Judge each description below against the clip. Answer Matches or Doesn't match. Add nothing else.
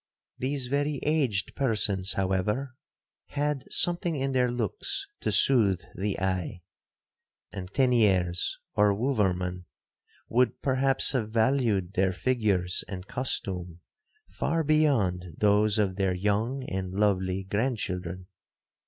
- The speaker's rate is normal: Doesn't match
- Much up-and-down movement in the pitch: Matches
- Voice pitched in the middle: Doesn't match